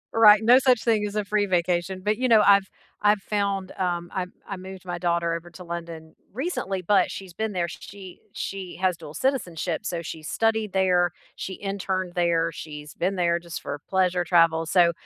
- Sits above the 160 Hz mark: Yes, medium, 185 Hz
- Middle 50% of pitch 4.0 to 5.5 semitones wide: No, average, 2.9 semitones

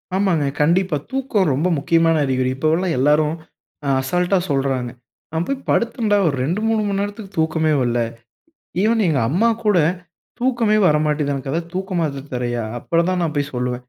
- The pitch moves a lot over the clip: Yes, wide, 5.9 semitones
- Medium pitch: Yes, medium, 165 Hz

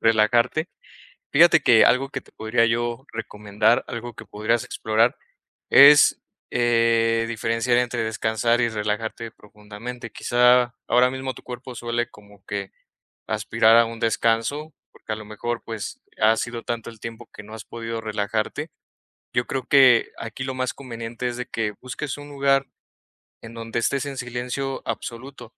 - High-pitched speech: No, low, 115 Hz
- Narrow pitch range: Yes, narrow, 1.9 semitones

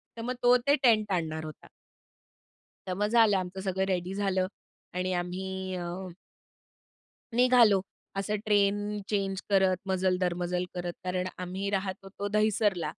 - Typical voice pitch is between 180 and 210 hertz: Yes, high, 190 Hz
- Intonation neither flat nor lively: No, narrow, 2.1 semitones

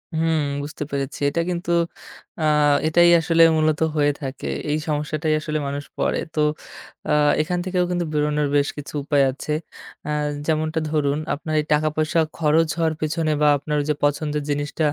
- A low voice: No, medium, 155 Hz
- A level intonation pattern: Yes, narrow, 1.5 semitones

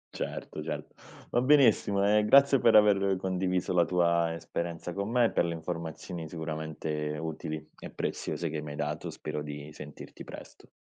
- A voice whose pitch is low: Yes, very low, 85 Hz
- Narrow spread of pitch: No, average, 4.1 semitones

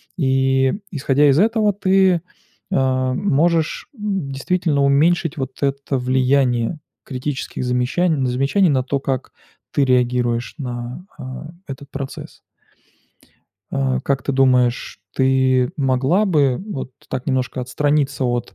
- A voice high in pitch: No, low, 135 Hz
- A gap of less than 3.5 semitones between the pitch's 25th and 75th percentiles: Yes, average, 3.0 semitones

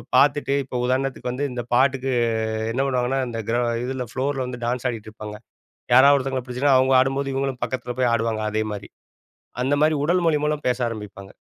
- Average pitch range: No, narrow, 2.0 semitones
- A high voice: No, low, 130 Hz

